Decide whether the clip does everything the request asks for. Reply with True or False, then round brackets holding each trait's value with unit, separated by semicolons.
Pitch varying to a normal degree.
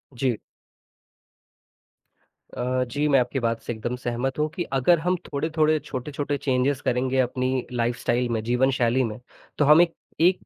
True (3.1 semitones)